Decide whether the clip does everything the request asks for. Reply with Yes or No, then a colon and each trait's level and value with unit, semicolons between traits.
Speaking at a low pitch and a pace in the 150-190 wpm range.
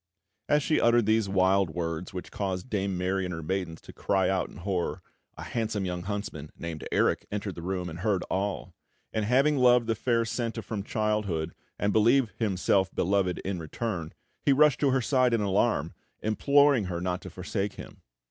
Yes: low, 100 Hz; average, 185 wpm